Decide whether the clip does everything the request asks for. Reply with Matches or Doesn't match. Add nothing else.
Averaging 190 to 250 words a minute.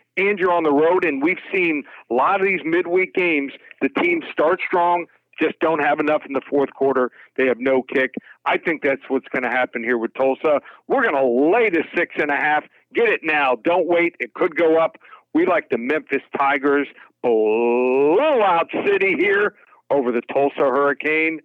Matches